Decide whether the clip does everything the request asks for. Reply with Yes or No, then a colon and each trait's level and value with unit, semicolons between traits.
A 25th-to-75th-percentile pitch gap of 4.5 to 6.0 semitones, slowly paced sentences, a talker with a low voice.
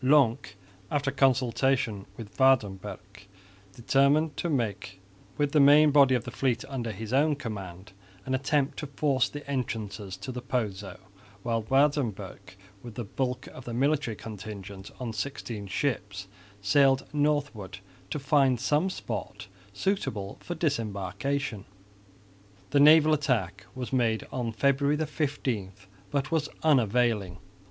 Yes: average, 5.3 semitones; slow, 130 wpm; low, 125 Hz